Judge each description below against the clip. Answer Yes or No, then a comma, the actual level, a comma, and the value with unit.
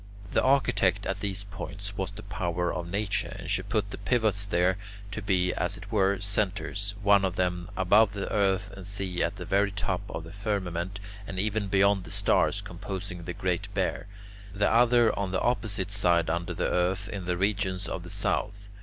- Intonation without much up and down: Yes, narrow, 1.9 semitones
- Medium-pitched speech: No, low, 100 Hz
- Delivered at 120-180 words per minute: No, average, 195 wpm